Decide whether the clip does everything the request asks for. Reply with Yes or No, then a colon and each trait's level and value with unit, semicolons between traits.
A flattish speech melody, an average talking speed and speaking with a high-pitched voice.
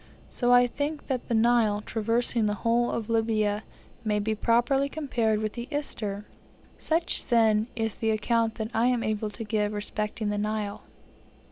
Yes: narrow, 2.2 semitones; average, 165 wpm; high, 225 Hz